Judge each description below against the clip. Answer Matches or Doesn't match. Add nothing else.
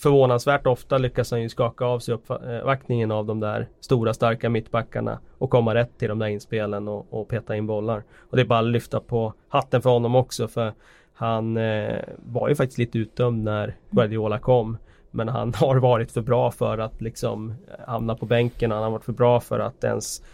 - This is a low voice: Matches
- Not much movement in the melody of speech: Matches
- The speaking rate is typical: Doesn't match